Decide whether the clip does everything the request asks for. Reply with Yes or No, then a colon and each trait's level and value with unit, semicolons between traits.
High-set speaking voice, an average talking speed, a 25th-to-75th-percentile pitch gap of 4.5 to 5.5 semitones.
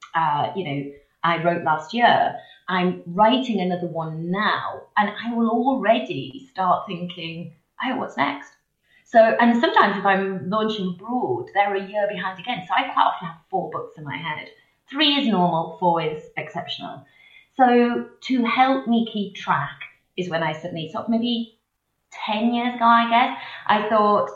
Yes: high, 210 Hz; average, 170 wpm; average, 5.2 semitones